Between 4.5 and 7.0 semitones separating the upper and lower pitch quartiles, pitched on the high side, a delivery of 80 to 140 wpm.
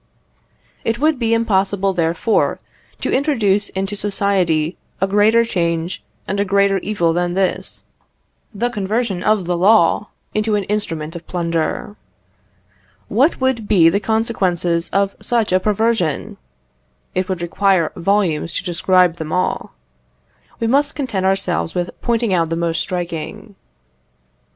No: average, 3.7 semitones; high, 195 Hz; slow, 135 wpm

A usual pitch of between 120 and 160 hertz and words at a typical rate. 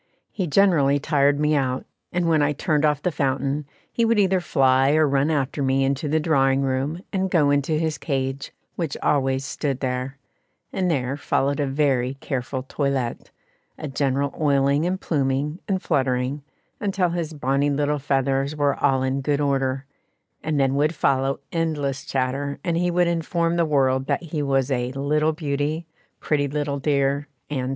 Yes: medium, 140 Hz; average, 170 wpm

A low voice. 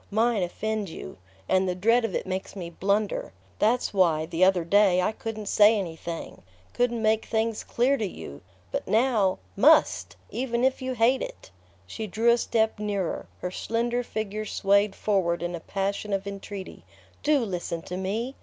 No: high, 205 Hz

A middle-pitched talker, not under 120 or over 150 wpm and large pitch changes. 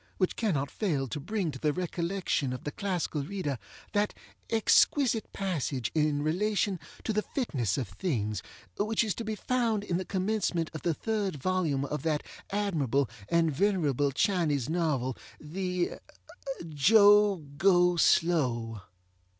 Yes: medium, 170 Hz; average, 140 wpm; wide, 5.9 semitones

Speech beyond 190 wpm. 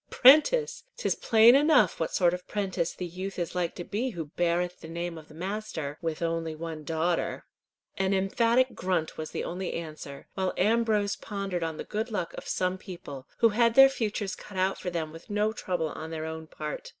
Yes: average, 200 wpm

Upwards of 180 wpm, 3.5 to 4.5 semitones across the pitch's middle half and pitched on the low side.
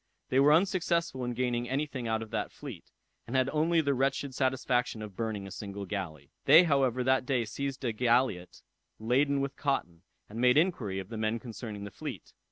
Yes: average, 195 wpm; average, 4.1 semitones; low, 125 Hz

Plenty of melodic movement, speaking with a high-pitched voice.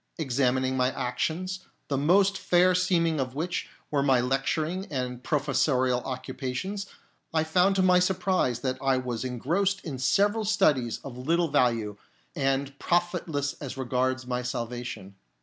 No: wide, 5.7 semitones; medium, 140 Hz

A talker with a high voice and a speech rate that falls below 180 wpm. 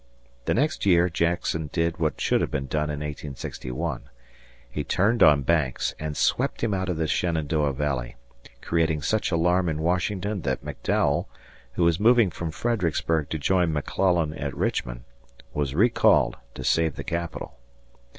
No: very low, 80 Hz; average, 155 wpm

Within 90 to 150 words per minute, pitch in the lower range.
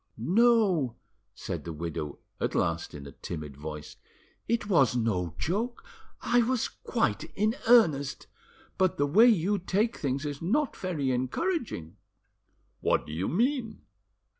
No: average, 140 wpm; medium, 160 Hz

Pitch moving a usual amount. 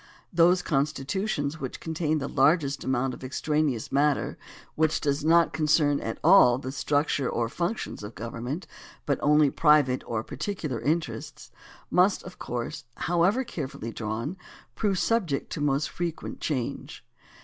Yes: average, 4.1 semitones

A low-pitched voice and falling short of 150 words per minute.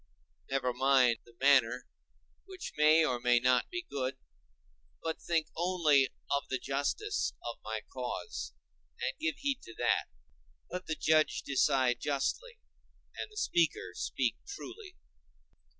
No: medium, 145 Hz; slow, 135 wpm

